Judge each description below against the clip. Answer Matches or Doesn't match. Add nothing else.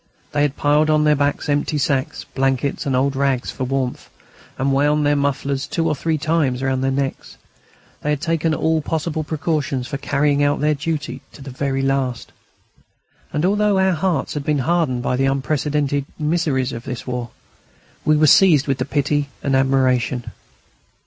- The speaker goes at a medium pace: Matches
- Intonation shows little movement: Matches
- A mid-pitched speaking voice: Matches